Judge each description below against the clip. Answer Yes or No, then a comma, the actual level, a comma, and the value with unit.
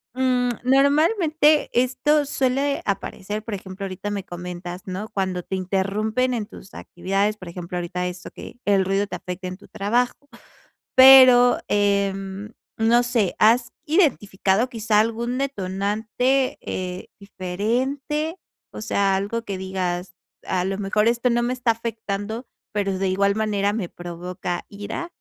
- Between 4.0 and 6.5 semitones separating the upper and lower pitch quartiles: Yes, average, 4.5 semitones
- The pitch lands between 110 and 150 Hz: No, high, 205 Hz